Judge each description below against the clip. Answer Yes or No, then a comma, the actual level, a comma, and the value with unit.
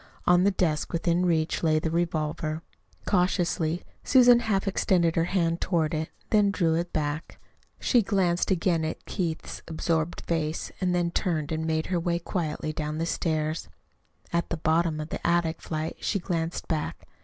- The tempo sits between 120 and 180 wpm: Yes, average, 165 wpm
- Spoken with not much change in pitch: Yes, narrow, 2.0 semitones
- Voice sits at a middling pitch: Yes, medium, 170 Hz